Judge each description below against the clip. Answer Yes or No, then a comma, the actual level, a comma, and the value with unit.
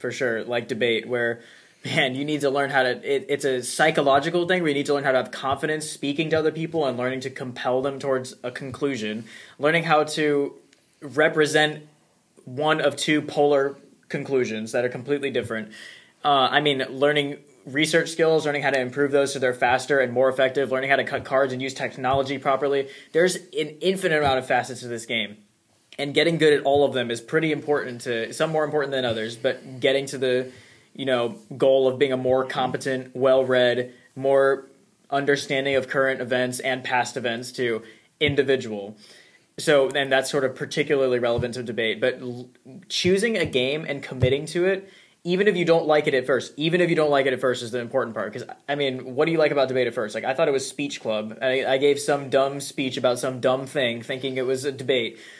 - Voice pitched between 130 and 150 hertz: Yes, low, 135 Hz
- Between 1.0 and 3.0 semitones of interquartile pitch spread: Yes, narrow, 2.5 semitones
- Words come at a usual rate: No, fast, 210 wpm